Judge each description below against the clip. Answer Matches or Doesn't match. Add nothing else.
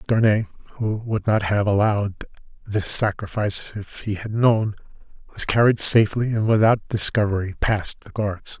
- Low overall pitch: Matches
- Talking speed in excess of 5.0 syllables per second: Doesn't match